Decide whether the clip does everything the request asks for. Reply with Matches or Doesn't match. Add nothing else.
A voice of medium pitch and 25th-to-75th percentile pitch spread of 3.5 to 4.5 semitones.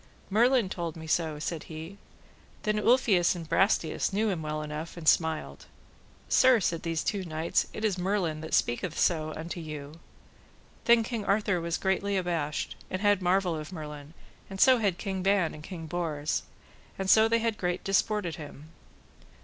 Matches